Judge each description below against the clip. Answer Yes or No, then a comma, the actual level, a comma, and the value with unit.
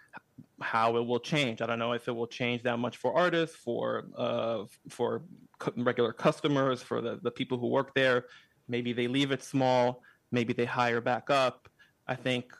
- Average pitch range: No, narrow, 1.7 semitones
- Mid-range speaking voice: No, low, 125 Hz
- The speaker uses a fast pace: No, average, 185 wpm